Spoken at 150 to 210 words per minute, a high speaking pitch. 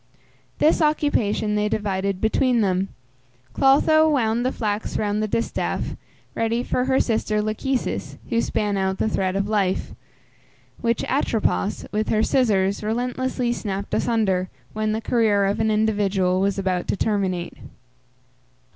No: average, 140 wpm; high, 215 Hz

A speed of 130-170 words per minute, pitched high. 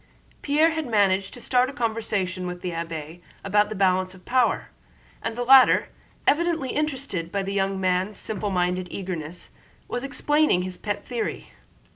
Yes: average, 160 wpm; high, 200 Hz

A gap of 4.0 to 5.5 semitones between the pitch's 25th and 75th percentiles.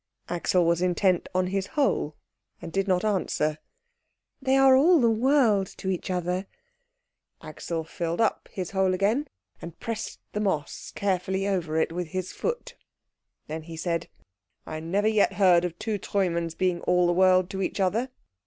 No: average, 3.3 semitones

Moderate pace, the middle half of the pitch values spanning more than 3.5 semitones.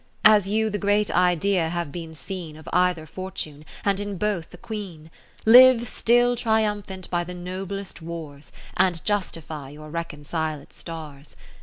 Yes: average, 145 wpm; average, 4.2 semitones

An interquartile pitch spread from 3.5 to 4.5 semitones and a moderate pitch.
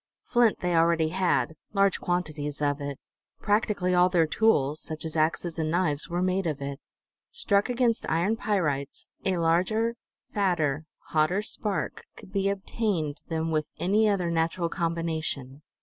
Yes: average, 4.1 semitones; medium, 170 Hz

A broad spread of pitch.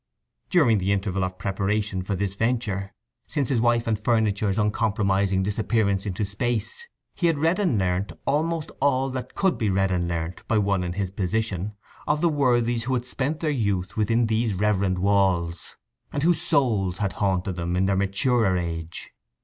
No: average, 4.2 semitones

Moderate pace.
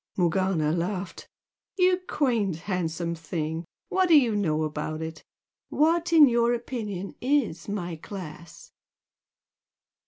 No: slow, 115 wpm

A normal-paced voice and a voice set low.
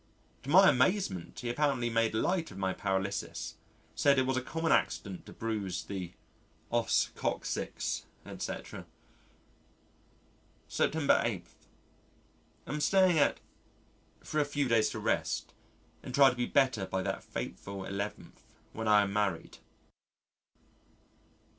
No: slow, 130 wpm; low, 115 Hz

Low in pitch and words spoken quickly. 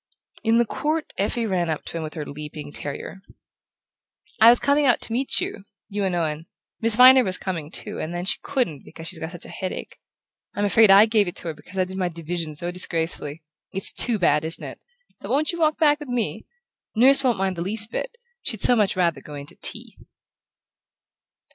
No: high, 190 Hz; fast, 215 wpm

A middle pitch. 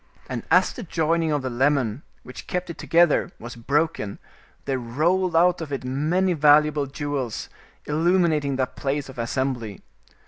Yes: medium, 145 Hz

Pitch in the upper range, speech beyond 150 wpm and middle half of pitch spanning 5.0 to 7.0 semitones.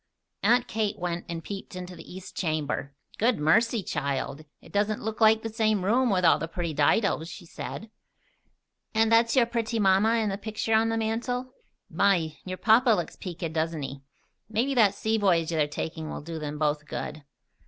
Yes: high, 200 Hz; average, 190 wpm; wide, 5.4 semitones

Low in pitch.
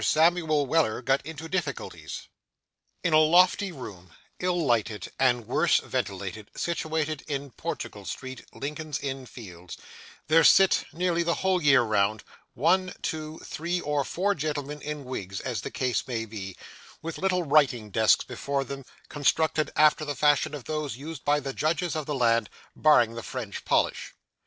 No: medium, 145 Hz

